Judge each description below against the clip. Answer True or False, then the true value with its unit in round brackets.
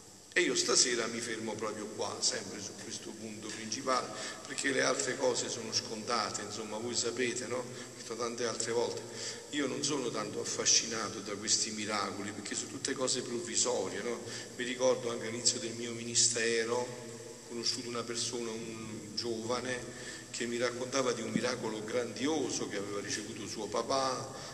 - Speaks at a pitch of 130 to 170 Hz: False (120 Hz)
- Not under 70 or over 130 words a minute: False (160 wpm)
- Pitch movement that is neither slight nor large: False (1.7 semitones)